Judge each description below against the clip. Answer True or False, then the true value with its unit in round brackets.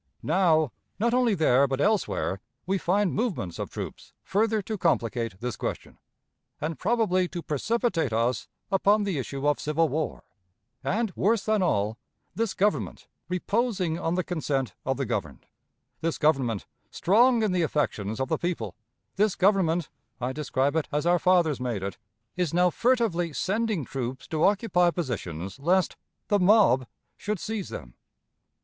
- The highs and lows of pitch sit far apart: True (6.9 semitones)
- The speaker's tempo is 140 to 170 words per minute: True (155 wpm)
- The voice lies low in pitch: False (170 Hz)